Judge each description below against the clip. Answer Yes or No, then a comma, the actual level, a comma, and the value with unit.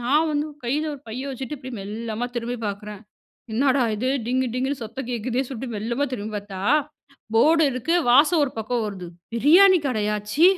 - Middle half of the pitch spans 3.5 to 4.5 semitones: Yes, average, 4.1 semitones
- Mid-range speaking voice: No, very high, 250 Hz